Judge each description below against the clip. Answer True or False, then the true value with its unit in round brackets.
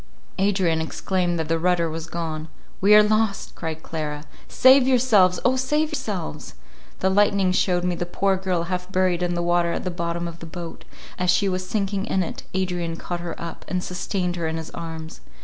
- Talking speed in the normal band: True (190 wpm)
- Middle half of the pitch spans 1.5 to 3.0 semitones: True (2.4 semitones)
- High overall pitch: False (180 Hz)